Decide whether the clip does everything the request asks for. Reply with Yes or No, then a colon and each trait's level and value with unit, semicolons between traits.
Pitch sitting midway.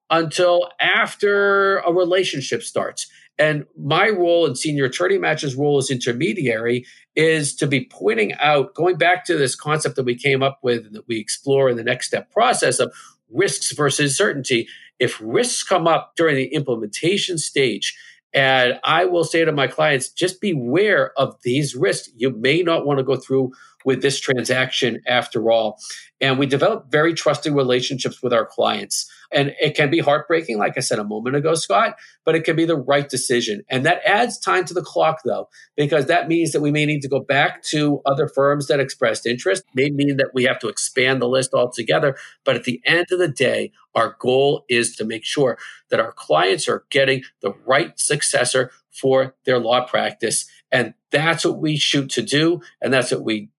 Yes: medium, 145 Hz